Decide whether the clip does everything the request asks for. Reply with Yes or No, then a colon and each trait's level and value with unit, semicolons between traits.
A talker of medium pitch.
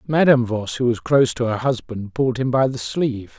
No: low, 125 Hz